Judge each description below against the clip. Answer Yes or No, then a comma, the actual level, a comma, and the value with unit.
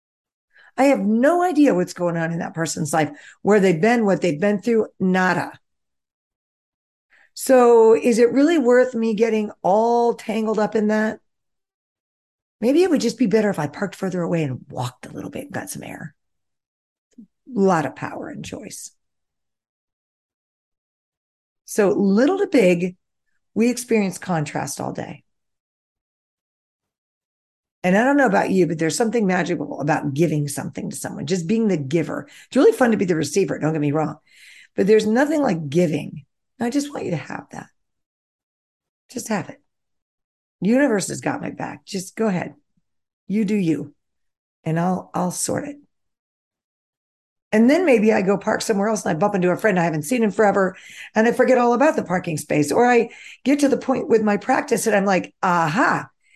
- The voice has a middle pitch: No, high, 205 Hz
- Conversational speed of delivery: Yes, average, 180 wpm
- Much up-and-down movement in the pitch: Yes, wide, 5.7 semitones